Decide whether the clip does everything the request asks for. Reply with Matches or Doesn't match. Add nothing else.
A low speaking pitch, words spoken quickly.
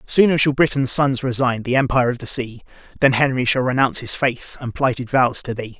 Matches